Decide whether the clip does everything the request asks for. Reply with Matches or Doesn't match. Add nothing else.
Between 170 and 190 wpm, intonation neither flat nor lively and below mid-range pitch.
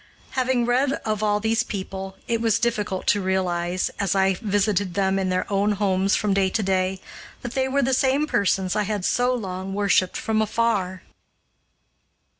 Doesn't match